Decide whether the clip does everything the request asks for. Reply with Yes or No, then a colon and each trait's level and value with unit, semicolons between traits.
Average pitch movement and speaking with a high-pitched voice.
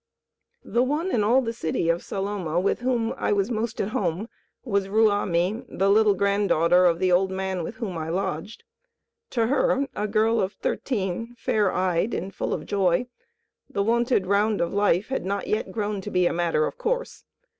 Yes: average, 3.7 semitones; high, 200 Hz